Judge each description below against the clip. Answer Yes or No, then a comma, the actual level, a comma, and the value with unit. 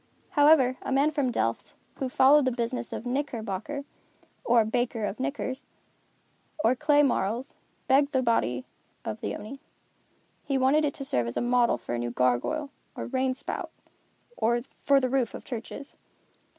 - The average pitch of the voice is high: Yes, very high, 255 Hz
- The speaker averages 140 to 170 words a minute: Yes, average, 165 wpm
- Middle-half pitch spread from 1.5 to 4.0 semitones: Yes, average, 3.5 semitones